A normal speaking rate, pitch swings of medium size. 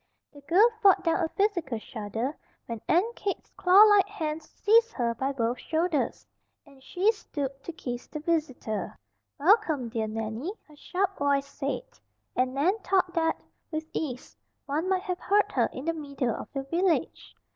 No: average, 165 wpm; wide, 5.8 semitones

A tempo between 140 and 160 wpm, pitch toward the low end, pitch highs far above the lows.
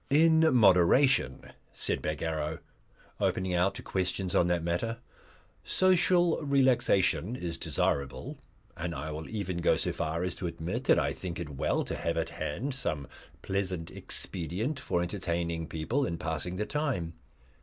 Yes: average, 150 wpm; very low, 90 Hz; wide, 6.2 semitones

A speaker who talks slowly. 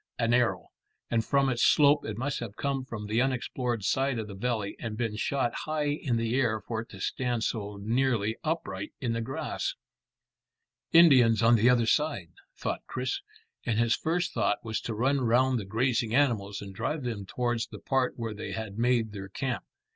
No: average, 190 wpm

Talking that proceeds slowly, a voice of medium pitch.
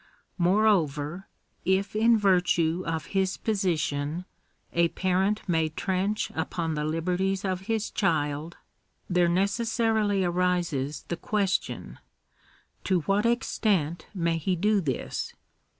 Yes: slow, 115 wpm; medium, 180 Hz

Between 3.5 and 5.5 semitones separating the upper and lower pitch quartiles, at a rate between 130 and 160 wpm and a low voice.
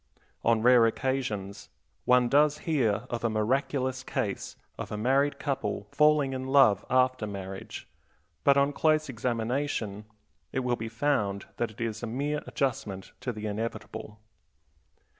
Yes: average, 4.2 semitones; average, 140 wpm; low, 125 Hz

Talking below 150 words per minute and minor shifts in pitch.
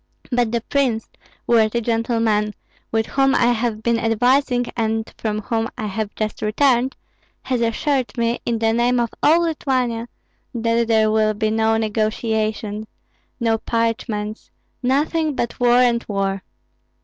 Yes: average, 140 wpm; narrow, 2.0 semitones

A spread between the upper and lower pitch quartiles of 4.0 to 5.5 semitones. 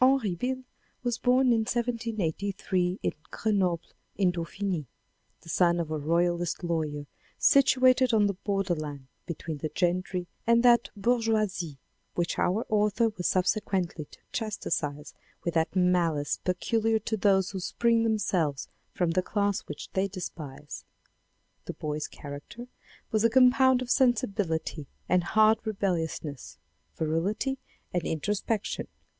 Yes: average, 5.0 semitones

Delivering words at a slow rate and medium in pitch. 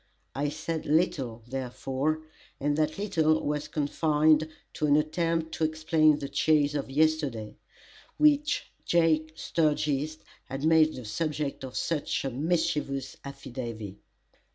Yes: slow, 125 wpm; medium, 150 Hz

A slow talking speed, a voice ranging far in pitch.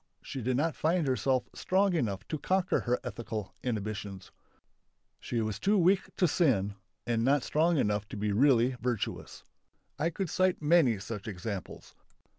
No: average, 155 wpm; wide, 7.3 semitones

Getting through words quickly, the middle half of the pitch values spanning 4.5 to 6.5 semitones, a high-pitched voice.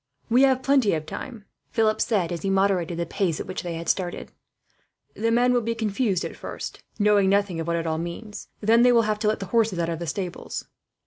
Yes: fast, 235 wpm; average, 4.9 semitones; high, 200 Hz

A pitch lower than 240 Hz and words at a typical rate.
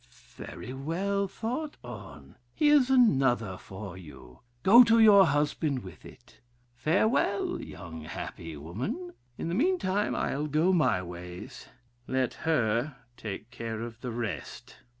No: low, 135 Hz; slow, 130 wpm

